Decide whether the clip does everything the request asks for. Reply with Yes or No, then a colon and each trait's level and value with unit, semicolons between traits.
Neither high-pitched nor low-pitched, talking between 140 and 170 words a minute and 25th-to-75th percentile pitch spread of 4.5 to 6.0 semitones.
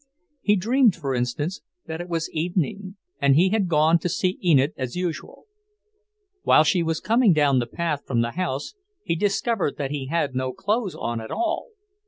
No: medium, 165 Hz; average, 185 wpm; average, 5.2 semitones